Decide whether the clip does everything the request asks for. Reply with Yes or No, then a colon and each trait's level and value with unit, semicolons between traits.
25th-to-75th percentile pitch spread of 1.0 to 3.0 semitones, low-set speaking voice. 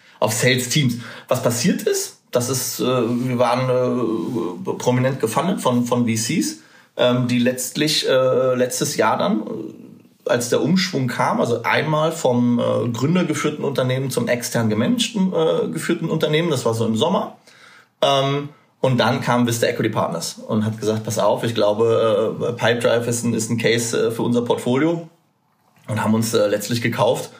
No: average, 4.3 semitones; low, 125 Hz